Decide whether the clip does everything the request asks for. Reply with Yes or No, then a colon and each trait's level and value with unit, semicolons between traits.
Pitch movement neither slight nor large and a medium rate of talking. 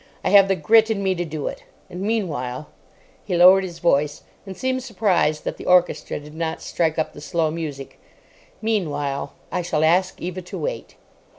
Yes: average, 4.0 semitones; average, 175 wpm